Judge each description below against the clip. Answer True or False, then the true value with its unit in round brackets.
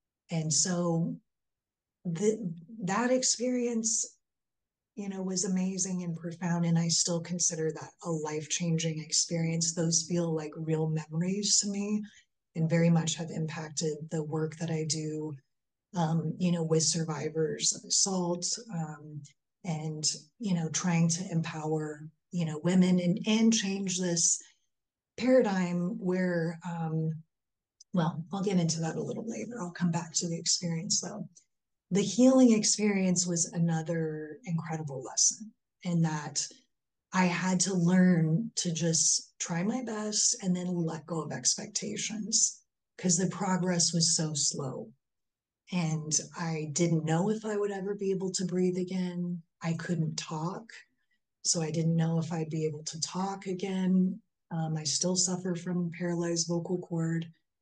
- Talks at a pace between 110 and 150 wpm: True (145 wpm)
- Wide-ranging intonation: False (2.8 semitones)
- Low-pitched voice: False (170 Hz)